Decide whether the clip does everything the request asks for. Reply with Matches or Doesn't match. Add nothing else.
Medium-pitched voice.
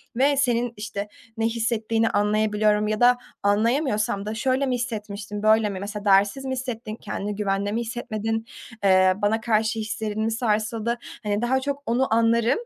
Doesn't match